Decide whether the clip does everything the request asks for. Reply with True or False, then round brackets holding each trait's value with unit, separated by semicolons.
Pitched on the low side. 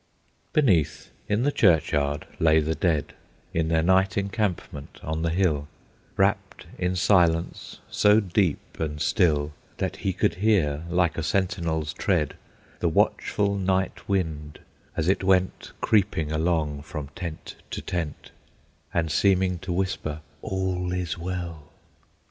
True (85 Hz)